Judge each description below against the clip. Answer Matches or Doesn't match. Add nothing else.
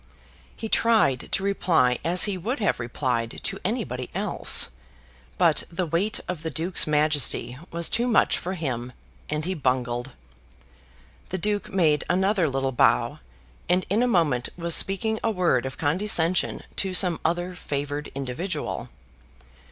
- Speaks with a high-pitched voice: Doesn't match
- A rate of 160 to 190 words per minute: Doesn't match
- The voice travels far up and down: Matches